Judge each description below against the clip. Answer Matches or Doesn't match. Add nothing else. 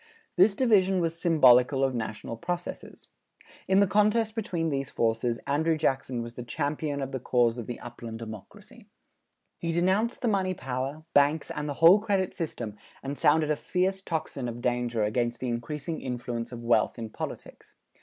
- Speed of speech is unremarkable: Matches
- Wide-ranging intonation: Matches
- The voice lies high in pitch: Doesn't match